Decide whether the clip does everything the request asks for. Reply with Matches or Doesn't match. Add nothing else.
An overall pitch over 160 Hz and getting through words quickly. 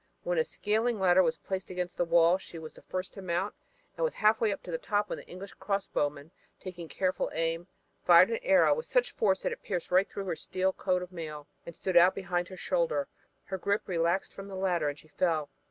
Matches